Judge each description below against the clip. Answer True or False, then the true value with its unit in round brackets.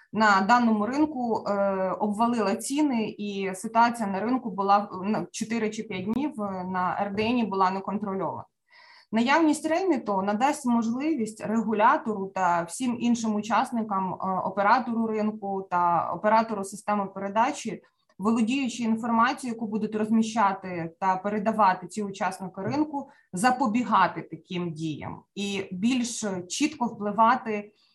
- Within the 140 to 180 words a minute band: False (115 wpm)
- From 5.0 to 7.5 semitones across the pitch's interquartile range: False (3.3 semitones)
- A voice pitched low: False (215 Hz)